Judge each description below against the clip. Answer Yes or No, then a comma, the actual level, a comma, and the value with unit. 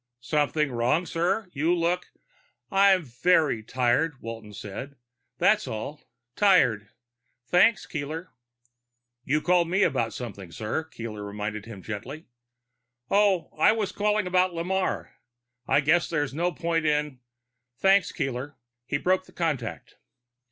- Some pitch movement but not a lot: No, wide, 6.8 semitones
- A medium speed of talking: No, slow, 130 wpm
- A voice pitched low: No, medium, 150 Hz